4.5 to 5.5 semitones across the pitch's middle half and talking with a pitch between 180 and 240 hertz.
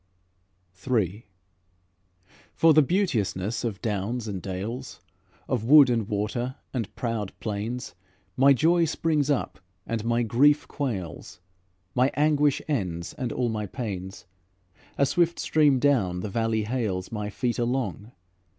No: average, 4.9 semitones; low, 120 Hz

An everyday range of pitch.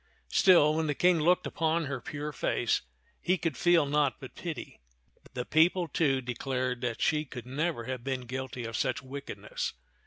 Yes: average, 4.1 semitones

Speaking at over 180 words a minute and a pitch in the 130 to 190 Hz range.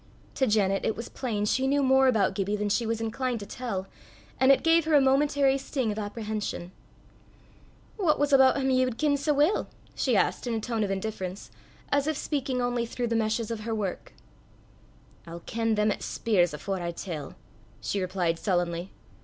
No: average, 195 wpm; high, 225 Hz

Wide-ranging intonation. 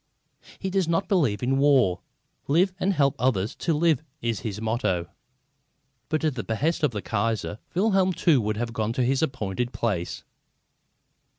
Yes: wide, 6.5 semitones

